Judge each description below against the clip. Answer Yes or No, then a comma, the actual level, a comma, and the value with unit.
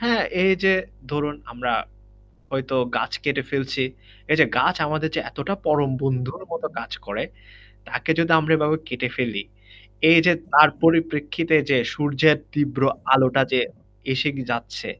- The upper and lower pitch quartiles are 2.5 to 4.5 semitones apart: Yes, average, 3.1 semitones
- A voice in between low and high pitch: Yes, medium, 145 Hz